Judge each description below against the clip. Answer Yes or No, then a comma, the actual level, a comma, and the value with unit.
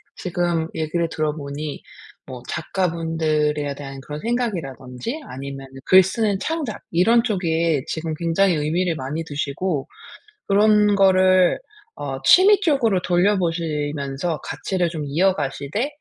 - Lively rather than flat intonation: No, average, 4.5 semitones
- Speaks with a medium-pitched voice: Yes, medium, 165 Hz